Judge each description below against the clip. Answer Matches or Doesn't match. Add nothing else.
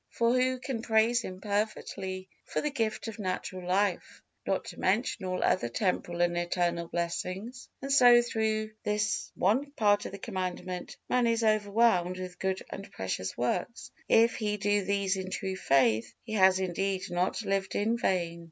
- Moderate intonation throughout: Matches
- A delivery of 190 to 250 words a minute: Doesn't match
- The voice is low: Doesn't match